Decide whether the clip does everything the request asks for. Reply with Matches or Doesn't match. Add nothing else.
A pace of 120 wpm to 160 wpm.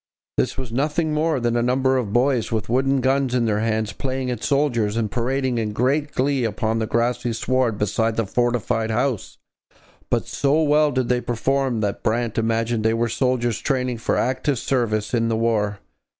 Doesn't match